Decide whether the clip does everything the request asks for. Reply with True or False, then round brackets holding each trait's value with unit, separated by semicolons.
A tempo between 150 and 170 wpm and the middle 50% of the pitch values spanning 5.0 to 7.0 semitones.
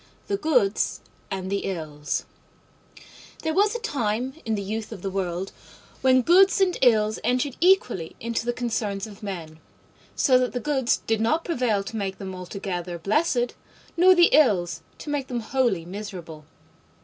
True (160 wpm; 5.6 semitones)